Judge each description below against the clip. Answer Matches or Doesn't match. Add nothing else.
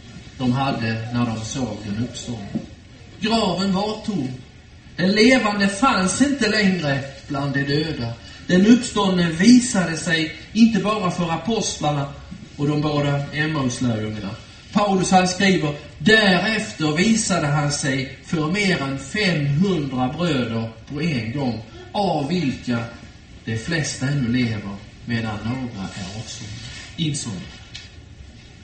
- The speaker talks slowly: Matches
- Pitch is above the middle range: Doesn't match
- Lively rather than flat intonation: Matches